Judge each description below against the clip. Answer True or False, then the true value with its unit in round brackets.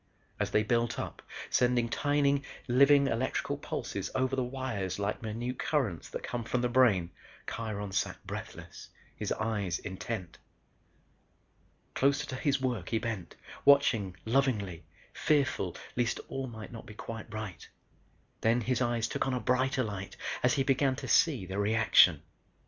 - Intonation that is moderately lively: True (3.8 semitones)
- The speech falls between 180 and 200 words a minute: False (150 wpm)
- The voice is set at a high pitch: False (120 Hz)